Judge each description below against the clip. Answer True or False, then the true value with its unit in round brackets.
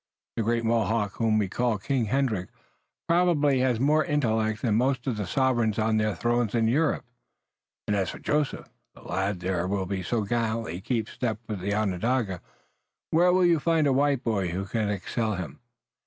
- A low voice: True (115 Hz)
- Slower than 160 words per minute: False (180 wpm)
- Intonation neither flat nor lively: True (4.3 semitones)